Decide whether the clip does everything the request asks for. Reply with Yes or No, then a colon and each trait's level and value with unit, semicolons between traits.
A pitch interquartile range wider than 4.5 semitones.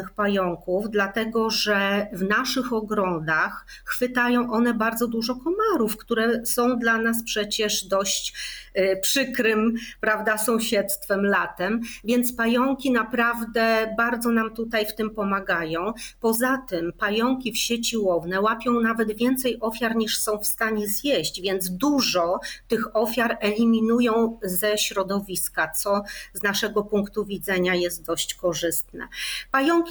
No: average, 2.9 semitones